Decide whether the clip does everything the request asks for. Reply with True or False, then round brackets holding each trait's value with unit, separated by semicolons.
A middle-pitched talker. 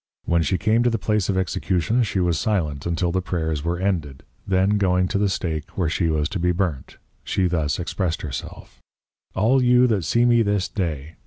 False (90 Hz)